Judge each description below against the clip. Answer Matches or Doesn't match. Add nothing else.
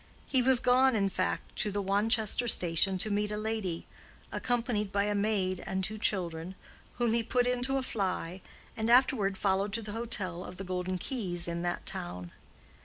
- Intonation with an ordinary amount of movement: Matches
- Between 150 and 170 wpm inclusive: Doesn't match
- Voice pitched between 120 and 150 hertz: Doesn't match